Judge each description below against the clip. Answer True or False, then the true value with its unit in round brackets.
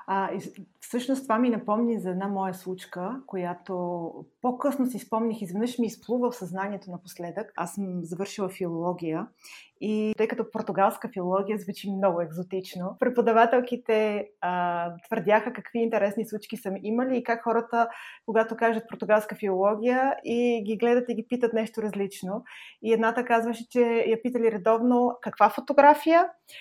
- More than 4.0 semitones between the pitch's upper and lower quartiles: False (3.3 semitones)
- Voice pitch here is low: False (220 Hz)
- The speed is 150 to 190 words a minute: False (140 wpm)